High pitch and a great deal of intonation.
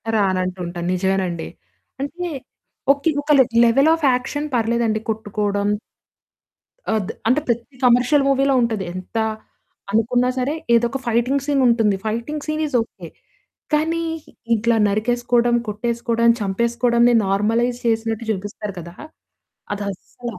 No: high, 235 Hz; average, 3.3 semitones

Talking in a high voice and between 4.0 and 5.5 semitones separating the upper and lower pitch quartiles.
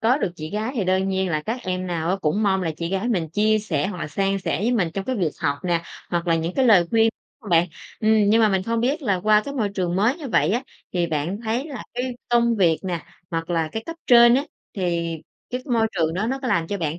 Yes: high, 195 Hz; average, 5.1 semitones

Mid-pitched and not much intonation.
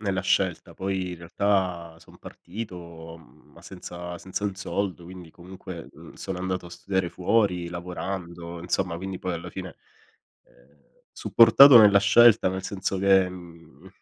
No: very low, 90 Hz; narrow, 1.9 semitones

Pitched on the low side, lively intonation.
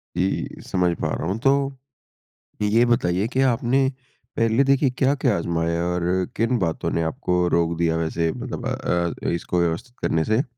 Yes: very low, 95 Hz; wide, 6.8 semitones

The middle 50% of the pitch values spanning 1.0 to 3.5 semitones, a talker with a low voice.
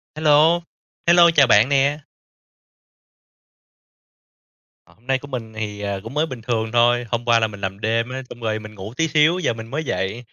No: average, 4.8 semitones; low, 120 Hz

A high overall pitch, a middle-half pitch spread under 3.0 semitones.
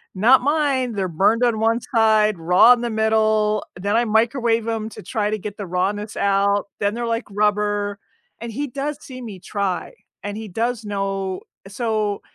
Yes: high, 215 Hz; narrow, 2.4 semitones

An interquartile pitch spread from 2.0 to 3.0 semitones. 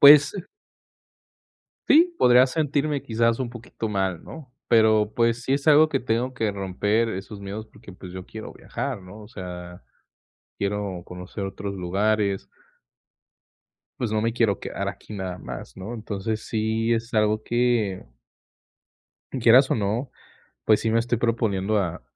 No: average, 3.4 semitones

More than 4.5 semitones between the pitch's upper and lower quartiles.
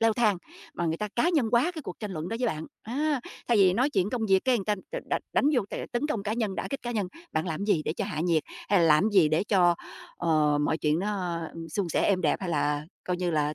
Yes: wide, 5.4 semitones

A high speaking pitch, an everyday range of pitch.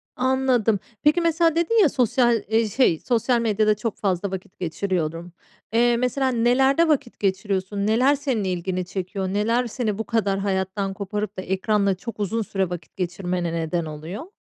Yes: high, 210 Hz; average, 4.5 semitones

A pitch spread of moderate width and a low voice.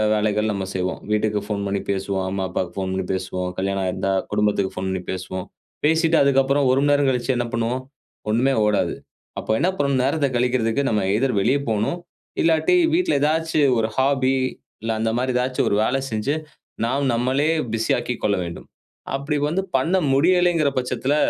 No: wide, 5.7 semitones; low, 120 Hz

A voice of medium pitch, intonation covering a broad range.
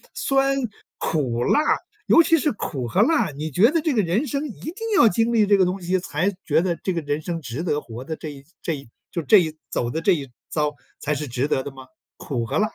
Yes: medium, 165 Hz; wide, 6.8 semitones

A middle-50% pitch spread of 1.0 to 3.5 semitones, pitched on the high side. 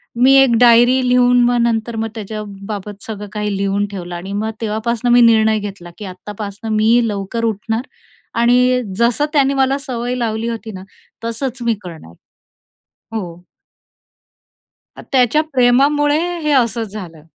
Yes: average, 3.1 semitones; high, 225 Hz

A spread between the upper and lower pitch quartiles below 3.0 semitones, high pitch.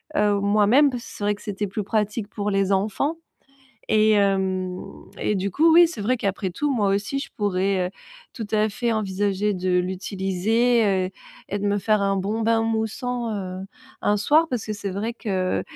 Yes: narrow, 2.5 semitones; high, 205 Hz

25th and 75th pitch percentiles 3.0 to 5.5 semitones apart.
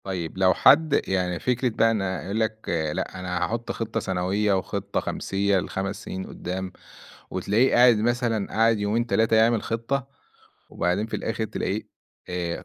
Yes: average, 3.3 semitones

